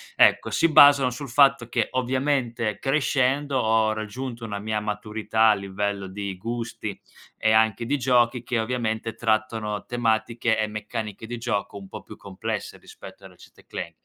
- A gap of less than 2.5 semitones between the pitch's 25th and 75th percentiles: No, average, 2.8 semitones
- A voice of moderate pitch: No, low, 115 Hz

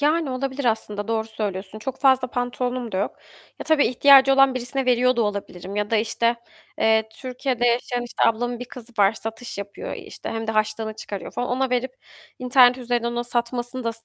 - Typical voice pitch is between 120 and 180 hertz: No, high, 240 Hz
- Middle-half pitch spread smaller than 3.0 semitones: Yes, narrow, 2.5 semitones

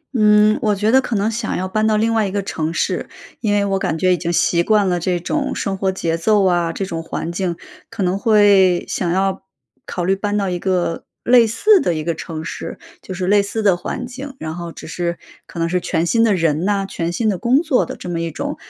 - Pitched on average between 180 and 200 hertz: Yes, high, 190 Hz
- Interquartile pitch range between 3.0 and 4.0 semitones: Yes, average, 3.6 semitones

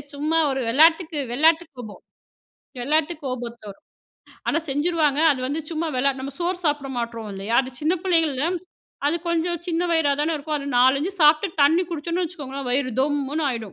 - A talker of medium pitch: No, very high, 295 Hz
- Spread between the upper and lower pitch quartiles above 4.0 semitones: No, average, 3.7 semitones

